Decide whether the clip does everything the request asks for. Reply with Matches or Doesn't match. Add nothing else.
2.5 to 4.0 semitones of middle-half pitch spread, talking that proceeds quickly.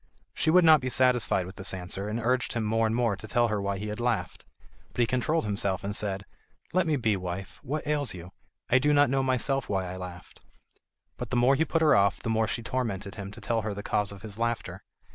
Doesn't match